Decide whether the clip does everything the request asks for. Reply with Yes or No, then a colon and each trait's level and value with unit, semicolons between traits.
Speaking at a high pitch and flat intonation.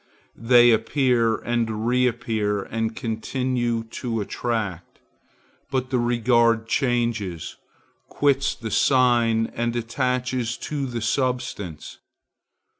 No: low, 120 Hz; narrow, 2.0 semitones